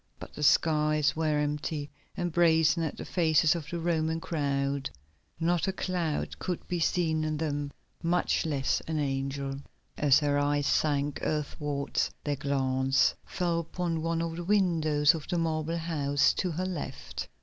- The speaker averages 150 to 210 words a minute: Yes, average, 160 wpm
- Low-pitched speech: No, medium, 155 Hz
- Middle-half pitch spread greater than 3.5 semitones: No, narrow, 2.5 semitones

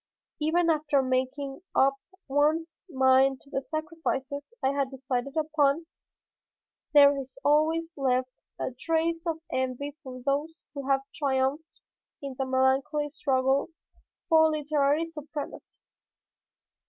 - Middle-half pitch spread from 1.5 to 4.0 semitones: Yes, average, 2.7 semitones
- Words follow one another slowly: Yes, slow, 115 wpm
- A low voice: No, very high, 280 Hz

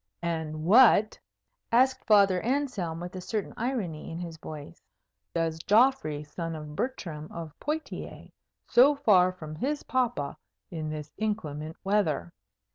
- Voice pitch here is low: No, medium, 180 Hz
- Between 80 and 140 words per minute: Yes, slow, 135 wpm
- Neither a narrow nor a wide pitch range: No, wide, 6.9 semitones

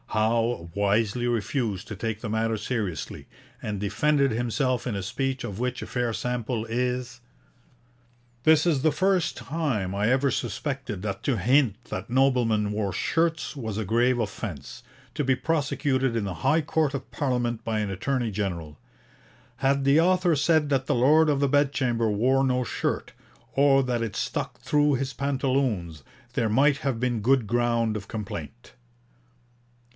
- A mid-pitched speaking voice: No, low, 120 Hz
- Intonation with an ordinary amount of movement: Yes, average, 4.2 semitones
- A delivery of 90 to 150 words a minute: No, average, 160 wpm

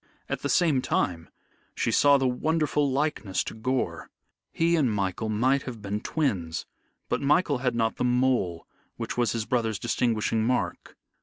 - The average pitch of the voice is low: Yes, low, 125 Hz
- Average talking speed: Yes, average, 160 wpm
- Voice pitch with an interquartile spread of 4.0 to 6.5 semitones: Yes, average, 4.4 semitones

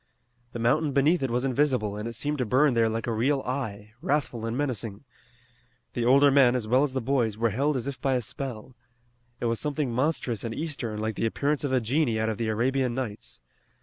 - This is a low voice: Yes, low, 125 Hz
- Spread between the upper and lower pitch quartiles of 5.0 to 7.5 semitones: No, average, 3.6 semitones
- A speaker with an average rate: No, fast, 220 wpm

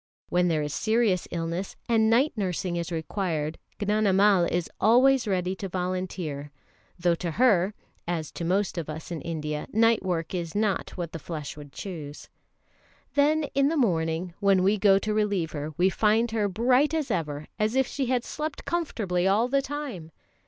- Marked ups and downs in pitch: No, average, 5.0 semitones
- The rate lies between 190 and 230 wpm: No, average, 175 wpm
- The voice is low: No, high, 190 Hz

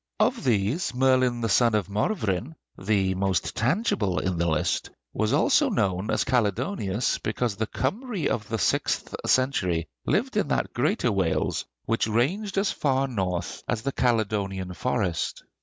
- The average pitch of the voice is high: No, low, 110 Hz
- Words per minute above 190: No, average, 150 wpm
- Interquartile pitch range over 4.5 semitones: Yes, average, 5.2 semitones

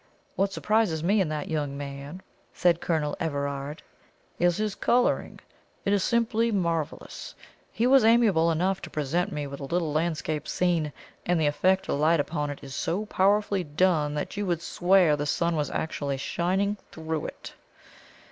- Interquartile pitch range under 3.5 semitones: No, average, 4.5 semitones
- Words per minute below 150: No, average, 165 wpm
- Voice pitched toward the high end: No, medium, 170 Hz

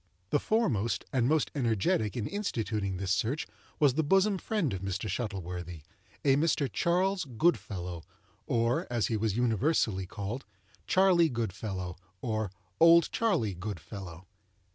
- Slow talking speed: Yes, slow, 125 wpm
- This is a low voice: Yes, low, 115 Hz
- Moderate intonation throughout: No, wide, 8.2 semitones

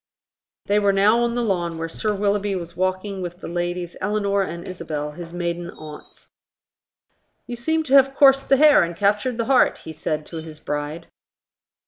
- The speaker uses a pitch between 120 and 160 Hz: No, medium, 185 Hz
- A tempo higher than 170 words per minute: Yes, average, 180 wpm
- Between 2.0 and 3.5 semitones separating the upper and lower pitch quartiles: No, average, 4.2 semitones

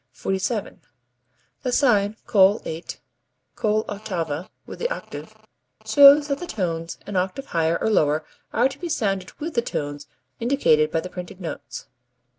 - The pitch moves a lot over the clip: Yes, wide, 7.1 semitones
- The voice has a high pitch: Yes, high, 200 Hz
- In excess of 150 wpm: No, average, 145 wpm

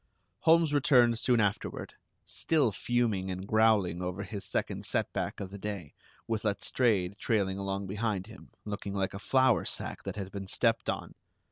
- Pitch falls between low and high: No, low, 105 Hz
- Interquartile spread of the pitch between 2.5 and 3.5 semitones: Yes, average, 3.1 semitones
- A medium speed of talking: Yes, average, 160 wpm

